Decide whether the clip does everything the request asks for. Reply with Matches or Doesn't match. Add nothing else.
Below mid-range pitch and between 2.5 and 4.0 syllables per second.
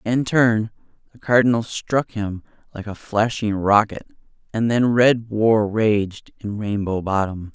Matches